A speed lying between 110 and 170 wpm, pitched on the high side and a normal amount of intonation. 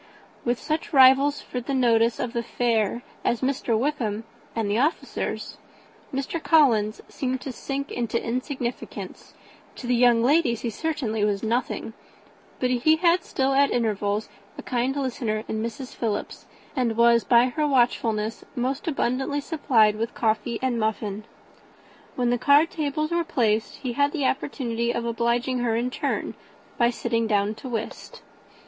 Yes: average, 155 wpm; high, 240 Hz; average, 3.1 semitones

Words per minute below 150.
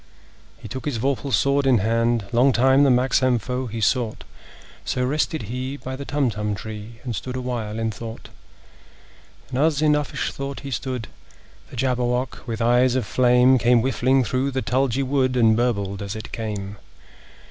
No: average, 170 wpm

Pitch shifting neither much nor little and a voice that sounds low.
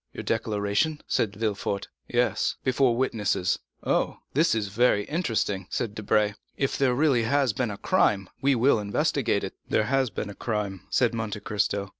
Yes: average, 3.8 semitones; low, 110 Hz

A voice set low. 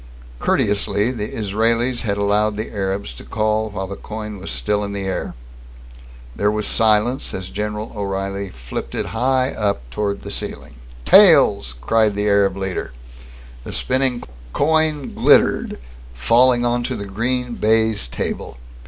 Yes: low, 105 Hz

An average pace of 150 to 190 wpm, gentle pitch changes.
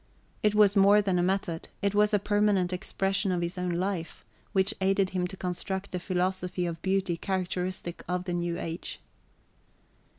Yes: average, 170 wpm; narrow, 1.8 semitones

